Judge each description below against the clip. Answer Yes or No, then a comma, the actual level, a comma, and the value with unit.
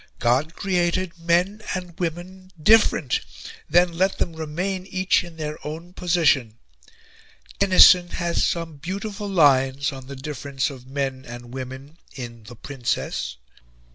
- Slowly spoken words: Yes, slow, 130 wpm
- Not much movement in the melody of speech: No, average, 5.2 semitones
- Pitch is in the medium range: Yes, medium, 165 Hz